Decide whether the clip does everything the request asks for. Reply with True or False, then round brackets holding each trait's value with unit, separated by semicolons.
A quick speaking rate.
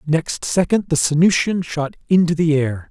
False (165 wpm)